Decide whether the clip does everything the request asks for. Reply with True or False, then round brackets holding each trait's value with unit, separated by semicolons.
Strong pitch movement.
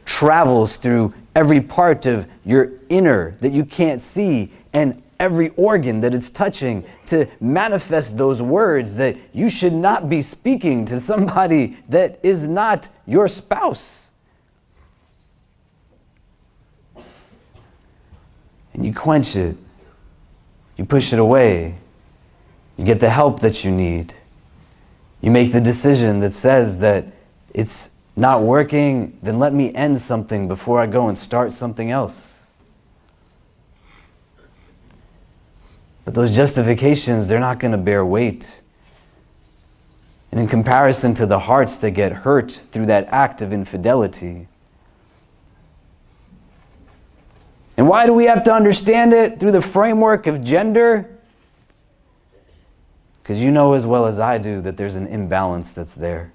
True (6.9 semitones)